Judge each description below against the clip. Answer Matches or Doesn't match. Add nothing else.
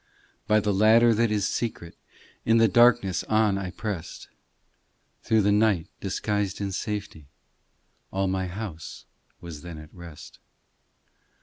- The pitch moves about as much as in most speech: Matches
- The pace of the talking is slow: Matches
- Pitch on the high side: Doesn't match